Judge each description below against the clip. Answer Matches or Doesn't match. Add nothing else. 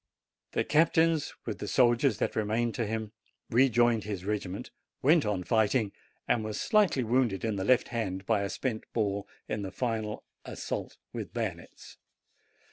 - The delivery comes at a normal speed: Matches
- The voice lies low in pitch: Matches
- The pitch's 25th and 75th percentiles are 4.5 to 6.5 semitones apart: Doesn't match